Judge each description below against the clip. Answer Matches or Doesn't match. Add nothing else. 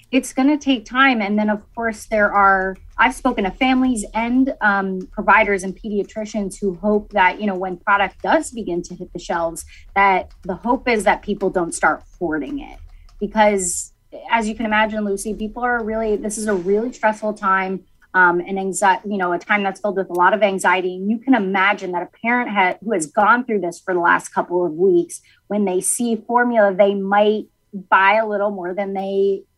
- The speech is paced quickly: Matches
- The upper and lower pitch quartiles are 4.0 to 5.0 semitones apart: Doesn't match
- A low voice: Doesn't match